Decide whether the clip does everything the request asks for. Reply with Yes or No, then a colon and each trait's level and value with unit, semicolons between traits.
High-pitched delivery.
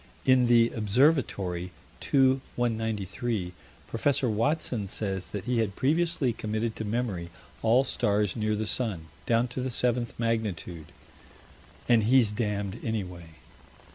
No: low, 110 Hz